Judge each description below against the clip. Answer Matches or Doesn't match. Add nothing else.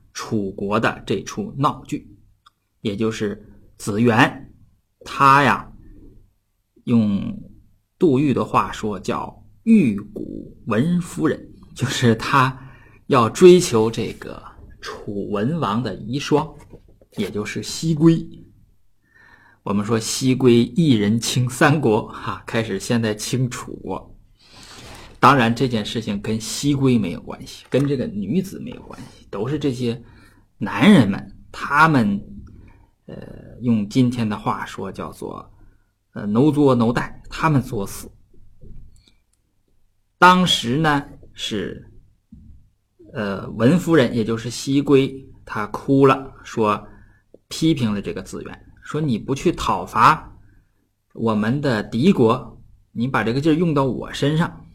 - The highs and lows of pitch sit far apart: Doesn't match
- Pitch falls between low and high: Doesn't match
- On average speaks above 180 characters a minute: Doesn't match